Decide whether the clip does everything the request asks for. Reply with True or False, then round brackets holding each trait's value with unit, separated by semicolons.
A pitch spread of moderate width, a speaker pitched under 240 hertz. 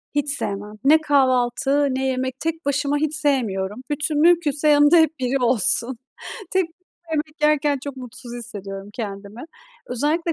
False (3.8 semitones; 275 Hz)